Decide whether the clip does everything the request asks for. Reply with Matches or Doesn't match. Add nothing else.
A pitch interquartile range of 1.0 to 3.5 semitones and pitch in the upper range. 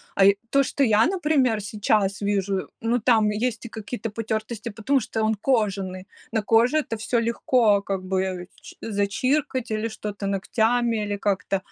Matches